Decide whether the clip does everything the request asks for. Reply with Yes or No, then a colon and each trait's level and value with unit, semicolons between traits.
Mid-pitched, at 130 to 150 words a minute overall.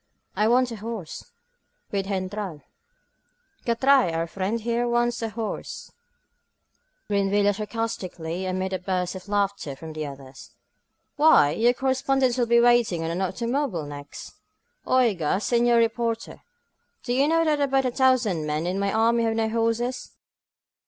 No: high, 220 Hz; average, 145 wpm